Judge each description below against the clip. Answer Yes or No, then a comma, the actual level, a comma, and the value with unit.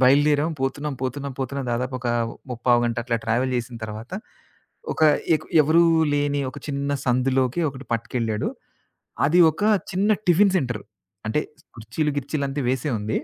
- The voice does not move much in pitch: No, average, 3.3 semitones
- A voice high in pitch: No, low, 135 Hz